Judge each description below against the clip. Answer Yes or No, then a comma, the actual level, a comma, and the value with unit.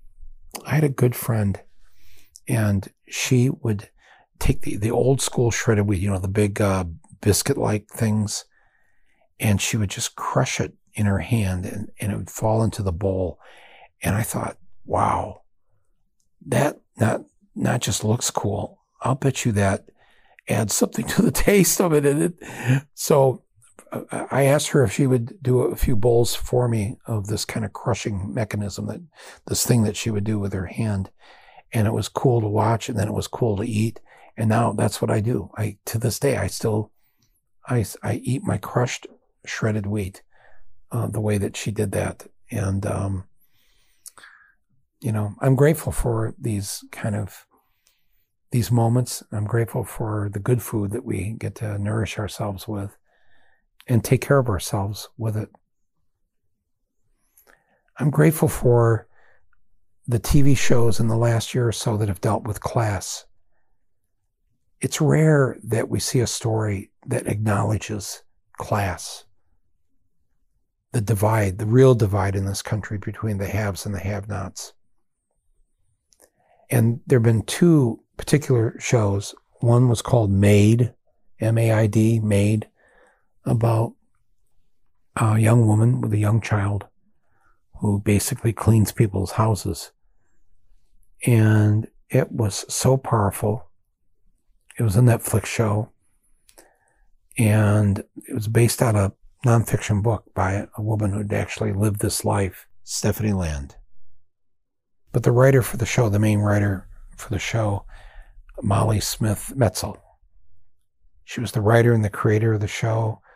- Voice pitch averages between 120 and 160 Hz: No, low, 110 Hz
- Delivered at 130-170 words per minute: Yes, average, 150 wpm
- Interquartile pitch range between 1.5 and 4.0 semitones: Yes, average, 2.9 semitones